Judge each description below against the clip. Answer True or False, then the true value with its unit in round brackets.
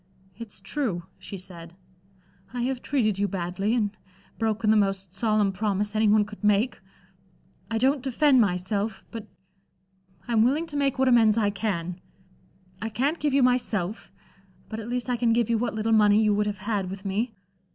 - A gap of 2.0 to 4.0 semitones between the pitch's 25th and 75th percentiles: True (3.2 semitones)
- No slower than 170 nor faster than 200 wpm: True (180 wpm)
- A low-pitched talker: False (215 Hz)